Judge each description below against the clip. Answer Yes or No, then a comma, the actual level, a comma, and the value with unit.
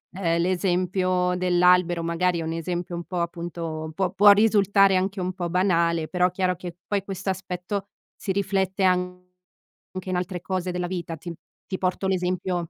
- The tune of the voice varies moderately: No, narrow, 1.5 semitones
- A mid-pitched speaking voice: Yes, medium, 180 Hz